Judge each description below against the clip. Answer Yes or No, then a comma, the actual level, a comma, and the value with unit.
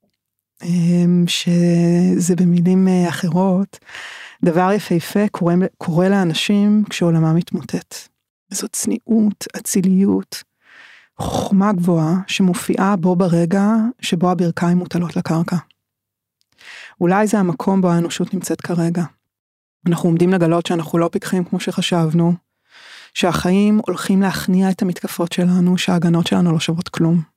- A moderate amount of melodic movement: No, narrow, 2.2 semitones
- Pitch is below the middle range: No, medium, 180 Hz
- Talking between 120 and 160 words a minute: No, average, 105 wpm